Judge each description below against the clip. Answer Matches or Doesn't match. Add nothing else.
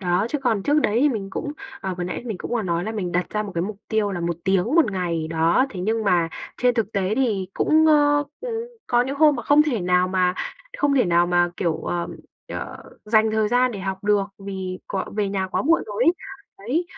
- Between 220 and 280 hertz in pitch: Doesn't match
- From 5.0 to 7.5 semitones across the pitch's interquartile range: Matches